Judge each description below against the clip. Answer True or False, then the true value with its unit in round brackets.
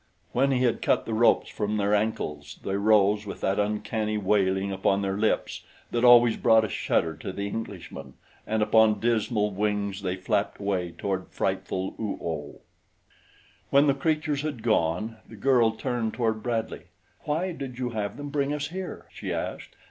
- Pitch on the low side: True (110 Hz)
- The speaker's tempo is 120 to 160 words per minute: False (170 wpm)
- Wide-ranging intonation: False (3.5 semitones)